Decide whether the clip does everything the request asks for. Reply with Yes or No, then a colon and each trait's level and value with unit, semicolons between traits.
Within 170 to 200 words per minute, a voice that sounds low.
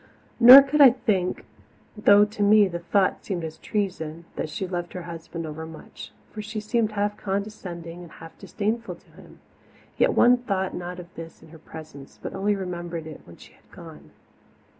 No: average, 180 wpm; medium, 185 Hz